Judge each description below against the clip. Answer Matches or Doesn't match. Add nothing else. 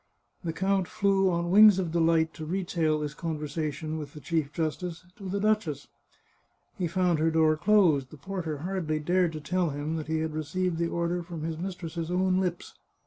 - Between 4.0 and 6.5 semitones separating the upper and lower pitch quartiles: Doesn't match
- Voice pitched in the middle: Matches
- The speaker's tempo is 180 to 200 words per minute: Matches